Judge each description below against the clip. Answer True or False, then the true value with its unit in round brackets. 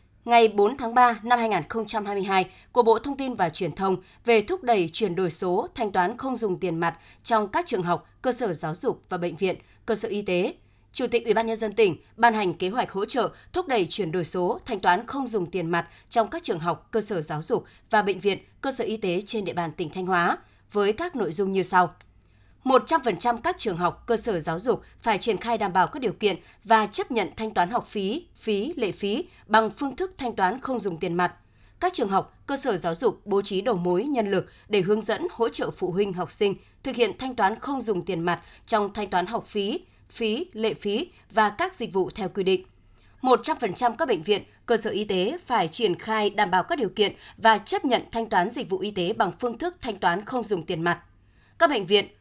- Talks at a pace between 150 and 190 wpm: False (240 wpm)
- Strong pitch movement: False (4.3 semitones)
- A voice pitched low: False (210 Hz)